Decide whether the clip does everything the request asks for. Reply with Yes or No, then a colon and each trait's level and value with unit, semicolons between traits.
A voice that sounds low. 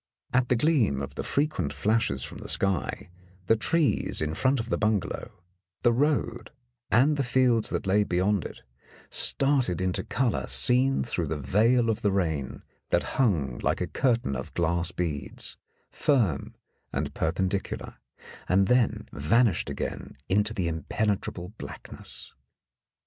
Yes: low, 105 Hz